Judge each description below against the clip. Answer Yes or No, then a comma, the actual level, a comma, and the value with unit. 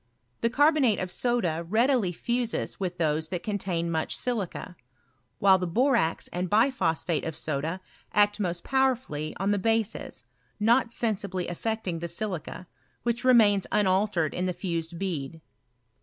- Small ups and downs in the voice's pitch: No, average, 5.1 semitones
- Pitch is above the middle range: Yes, high, 195 Hz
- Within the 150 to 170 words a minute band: No, average, 140 wpm